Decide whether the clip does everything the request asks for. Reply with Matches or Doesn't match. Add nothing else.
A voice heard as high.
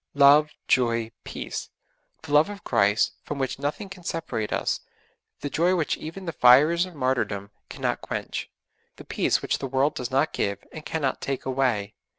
Doesn't match